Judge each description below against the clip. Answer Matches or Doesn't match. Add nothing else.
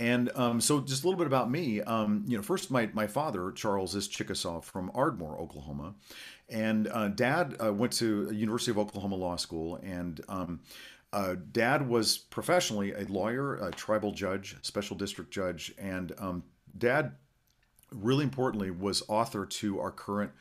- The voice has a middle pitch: Doesn't match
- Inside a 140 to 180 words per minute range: Matches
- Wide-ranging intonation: Doesn't match